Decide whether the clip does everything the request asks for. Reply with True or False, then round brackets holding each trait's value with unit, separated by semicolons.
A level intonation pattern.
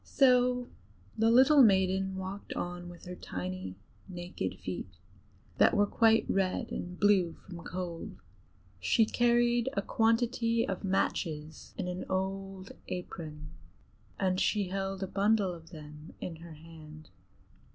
False (4.3 semitones)